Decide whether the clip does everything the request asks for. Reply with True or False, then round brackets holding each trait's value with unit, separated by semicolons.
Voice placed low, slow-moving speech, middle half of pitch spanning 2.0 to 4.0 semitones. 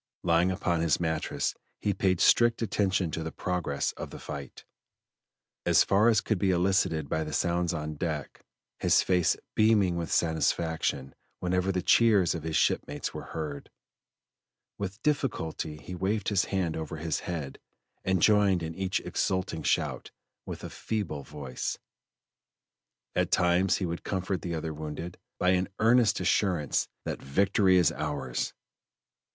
False (90 Hz; 150 wpm; 3.3 semitones)